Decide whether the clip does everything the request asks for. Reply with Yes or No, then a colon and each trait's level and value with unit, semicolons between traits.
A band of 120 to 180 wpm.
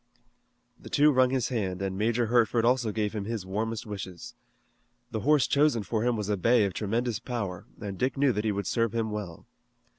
No: fast, 205 wpm